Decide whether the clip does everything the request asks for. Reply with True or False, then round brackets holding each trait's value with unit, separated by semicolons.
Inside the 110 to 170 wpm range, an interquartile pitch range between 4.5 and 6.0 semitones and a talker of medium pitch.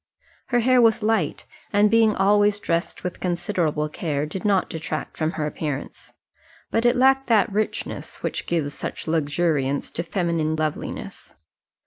True (145 wpm; 5.4 semitones; 175 Hz)